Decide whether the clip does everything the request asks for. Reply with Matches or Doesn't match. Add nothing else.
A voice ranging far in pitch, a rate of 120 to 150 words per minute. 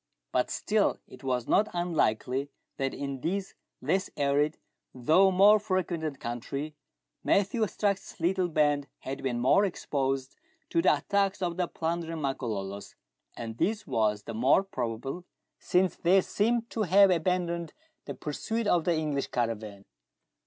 Matches